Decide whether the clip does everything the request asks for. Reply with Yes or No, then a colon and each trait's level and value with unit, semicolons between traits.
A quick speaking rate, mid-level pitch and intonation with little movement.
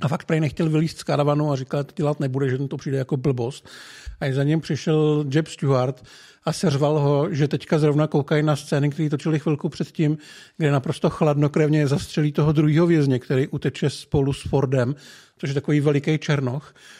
Yes: fast, 195 wpm; medium, 150 Hz; narrow, 1.6 semitones